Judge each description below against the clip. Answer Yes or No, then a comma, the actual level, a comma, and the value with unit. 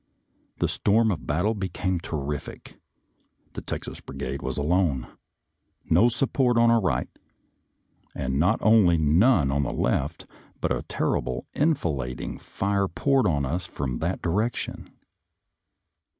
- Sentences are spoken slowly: Yes, slow, 125 wpm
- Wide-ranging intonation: Yes, wide, 7.3 semitones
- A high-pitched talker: No, very low, 85 Hz